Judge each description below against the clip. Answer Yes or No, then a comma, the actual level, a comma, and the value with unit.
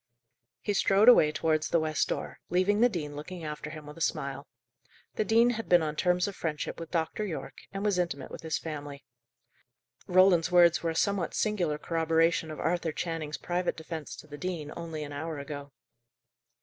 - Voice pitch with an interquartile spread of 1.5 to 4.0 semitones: Yes, average, 2.9 semitones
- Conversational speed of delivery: Yes, average, 190 wpm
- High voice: No, medium, 165 Hz